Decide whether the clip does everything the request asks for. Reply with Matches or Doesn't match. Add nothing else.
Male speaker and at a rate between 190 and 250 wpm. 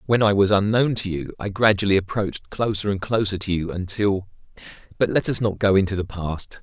Matches